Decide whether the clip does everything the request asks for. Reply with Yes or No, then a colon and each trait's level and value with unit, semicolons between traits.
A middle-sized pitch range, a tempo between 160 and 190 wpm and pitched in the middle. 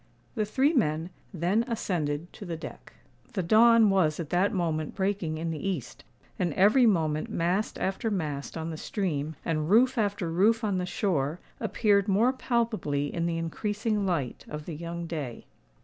Yes: average, 4.9 semitones; average, 170 wpm; medium, 180 Hz